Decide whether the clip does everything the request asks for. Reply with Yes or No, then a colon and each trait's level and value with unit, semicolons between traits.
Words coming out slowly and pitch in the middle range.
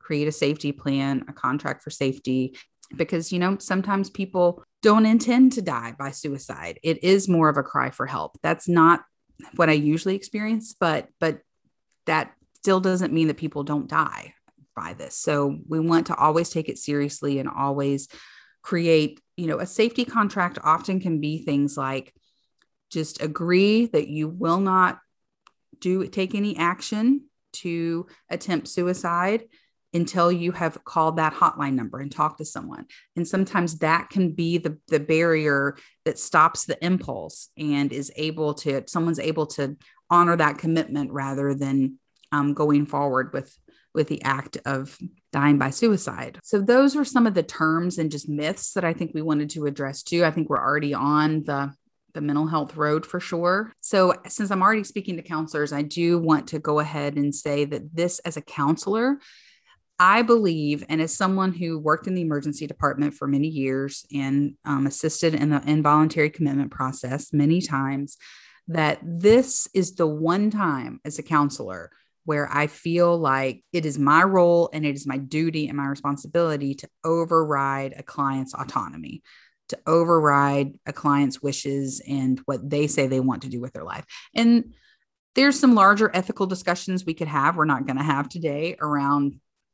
No: average, 175 wpm; medium, 155 Hz